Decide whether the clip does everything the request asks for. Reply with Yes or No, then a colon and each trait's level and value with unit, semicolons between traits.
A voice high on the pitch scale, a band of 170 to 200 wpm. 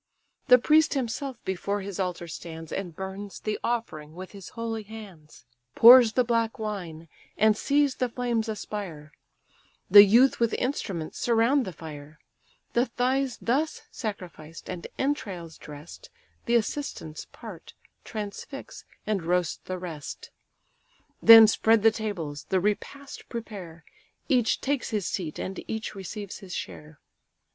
No: high, 210 Hz; slow, 135 wpm